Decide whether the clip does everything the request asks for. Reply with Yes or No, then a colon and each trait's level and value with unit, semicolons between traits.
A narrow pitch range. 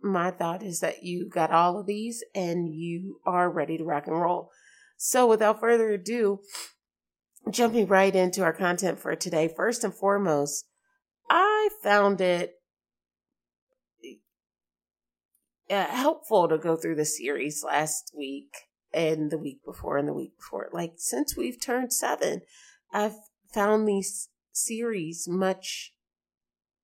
No: wide, 5.4 semitones